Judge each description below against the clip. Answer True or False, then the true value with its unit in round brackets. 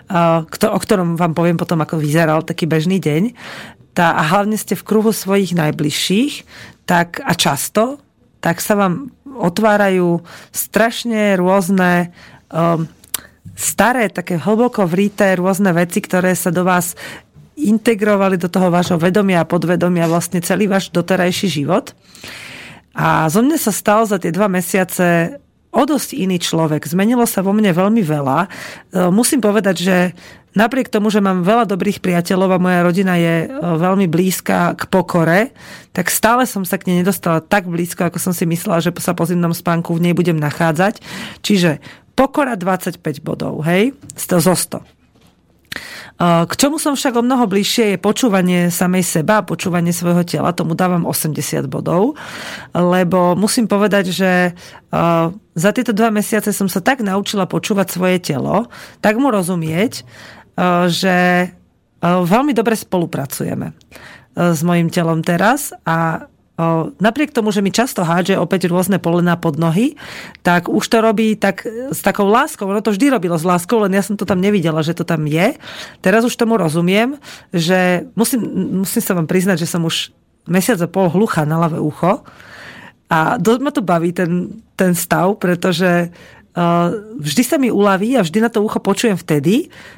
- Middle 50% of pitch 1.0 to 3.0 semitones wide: False (3.6 semitones)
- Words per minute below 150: False (160 wpm)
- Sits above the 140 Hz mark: True (185 Hz)